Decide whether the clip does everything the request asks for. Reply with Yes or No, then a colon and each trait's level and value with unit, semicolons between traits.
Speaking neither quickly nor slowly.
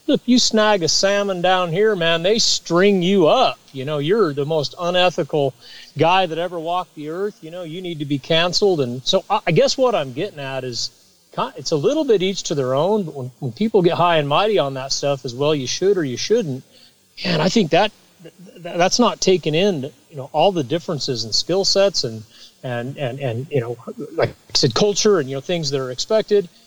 No: fast, 225 wpm